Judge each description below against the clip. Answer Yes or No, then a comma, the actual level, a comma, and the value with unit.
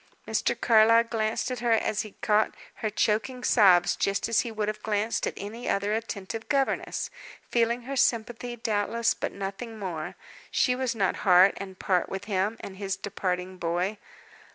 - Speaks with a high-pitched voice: Yes, high, 215 Hz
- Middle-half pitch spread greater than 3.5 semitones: No, average, 2.9 semitones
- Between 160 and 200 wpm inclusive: Yes, average, 170 wpm